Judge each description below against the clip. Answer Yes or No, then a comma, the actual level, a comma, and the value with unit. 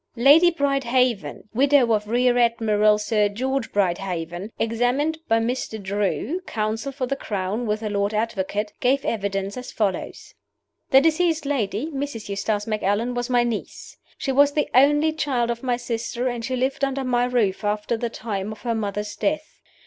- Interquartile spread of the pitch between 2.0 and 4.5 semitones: Yes, average, 4.2 semitones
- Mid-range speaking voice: No, high, 235 Hz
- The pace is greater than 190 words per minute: No, average, 165 wpm